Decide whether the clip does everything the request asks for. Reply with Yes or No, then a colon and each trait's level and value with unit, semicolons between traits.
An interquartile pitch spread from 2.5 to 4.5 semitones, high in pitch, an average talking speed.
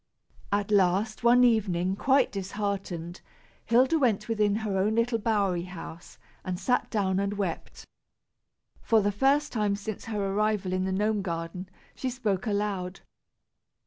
Yes: average, 2.8 semitones; high, 205 Hz; average, 145 wpm